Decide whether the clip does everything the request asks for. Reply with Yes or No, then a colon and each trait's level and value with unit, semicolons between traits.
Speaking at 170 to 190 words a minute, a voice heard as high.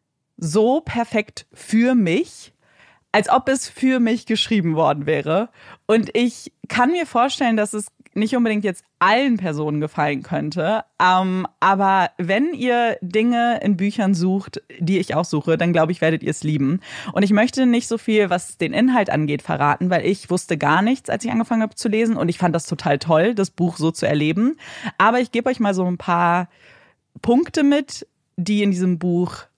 Yes: average, 185 wpm; high, 200 Hz